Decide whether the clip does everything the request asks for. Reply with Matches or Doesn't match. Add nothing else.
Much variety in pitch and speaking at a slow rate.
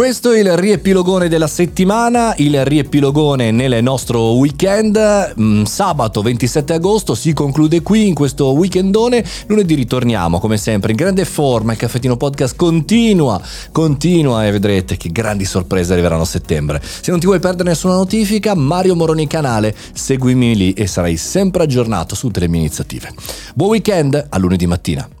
Doesn't match